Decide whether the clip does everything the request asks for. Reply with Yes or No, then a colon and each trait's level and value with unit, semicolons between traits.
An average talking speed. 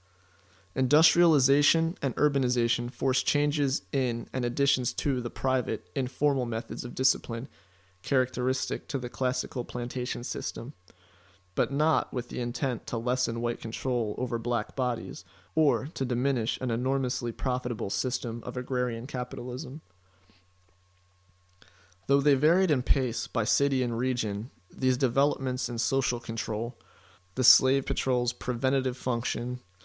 No: slow, 125 wpm